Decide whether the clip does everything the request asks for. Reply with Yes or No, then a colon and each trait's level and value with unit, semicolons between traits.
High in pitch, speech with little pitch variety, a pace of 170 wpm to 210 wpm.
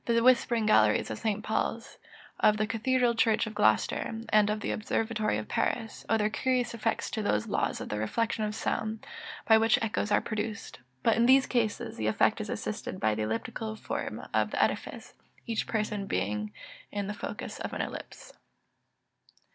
Yes: high, 215 Hz; narrow, 1.8 semitones; average, 180 wpm